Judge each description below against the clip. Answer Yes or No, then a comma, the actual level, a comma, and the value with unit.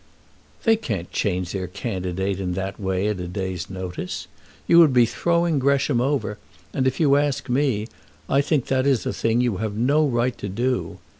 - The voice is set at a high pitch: No, low, 120 Hz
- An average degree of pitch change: No, wide, 6.5 semitones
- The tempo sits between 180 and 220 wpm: Yes, average, 190 wpm